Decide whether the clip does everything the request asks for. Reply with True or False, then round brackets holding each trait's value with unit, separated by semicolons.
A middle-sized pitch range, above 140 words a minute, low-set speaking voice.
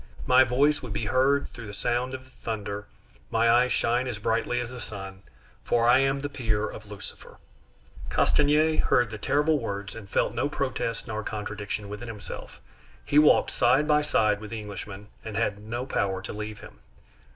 True (3.8 semitones; 185 wpm; 115 Hz)